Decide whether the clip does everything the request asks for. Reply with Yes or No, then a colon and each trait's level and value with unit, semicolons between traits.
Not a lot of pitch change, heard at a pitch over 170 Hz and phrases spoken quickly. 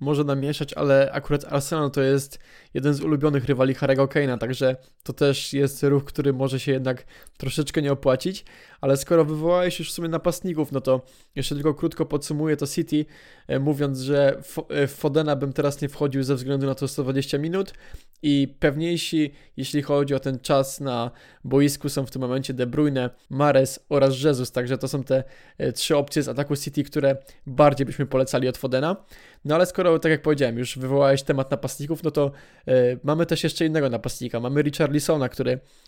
No: narrow, 2.1 semitones; medium, 140 Hz; fast, 180 wpm